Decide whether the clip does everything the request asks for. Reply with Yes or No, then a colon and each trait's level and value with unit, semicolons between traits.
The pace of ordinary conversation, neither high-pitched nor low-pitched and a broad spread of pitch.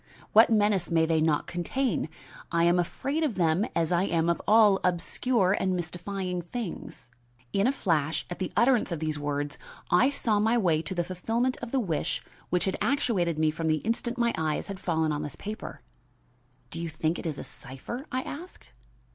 Yes: average, 190 wpm; medium, 180 Hz; wide, 5.7 semitones